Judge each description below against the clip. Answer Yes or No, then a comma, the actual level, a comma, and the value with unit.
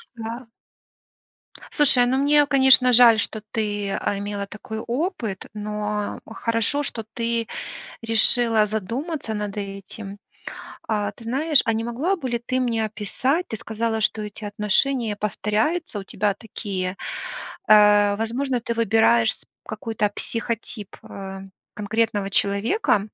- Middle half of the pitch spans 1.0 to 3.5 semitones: Yes, average, 2.7 semitones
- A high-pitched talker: Yes, high, 220 Hz